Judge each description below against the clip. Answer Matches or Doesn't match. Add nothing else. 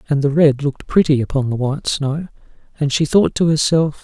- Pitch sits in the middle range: Matches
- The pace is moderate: Doesn't match